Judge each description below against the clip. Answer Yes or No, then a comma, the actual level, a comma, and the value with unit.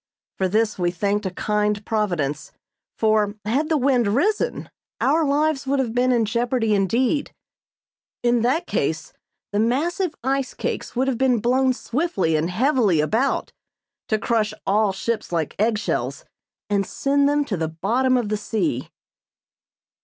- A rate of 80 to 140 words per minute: No, average, 155 wpm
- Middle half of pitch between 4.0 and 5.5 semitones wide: Yes, average, 4.5 semitones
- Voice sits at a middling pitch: No, high, 230 Hz